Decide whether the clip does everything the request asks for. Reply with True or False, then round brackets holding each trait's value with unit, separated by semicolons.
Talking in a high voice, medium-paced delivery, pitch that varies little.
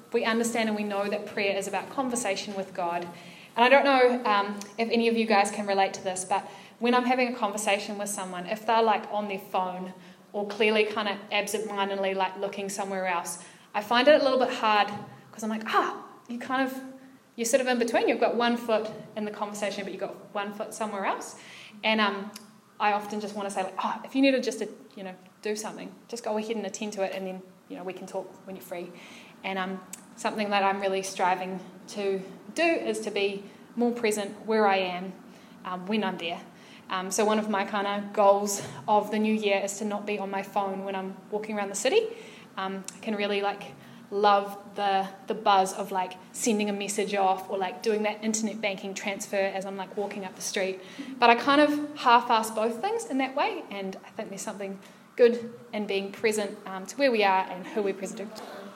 False (205 Hz; 225 wpm; 2.2 semitones)